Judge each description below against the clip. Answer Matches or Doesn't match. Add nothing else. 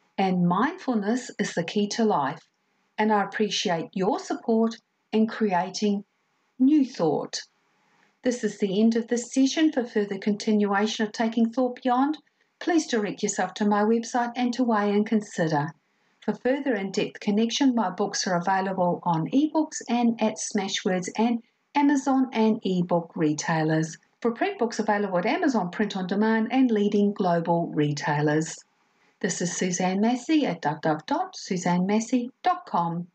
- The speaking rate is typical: Matches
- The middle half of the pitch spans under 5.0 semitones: Matches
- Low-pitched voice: Doesn't match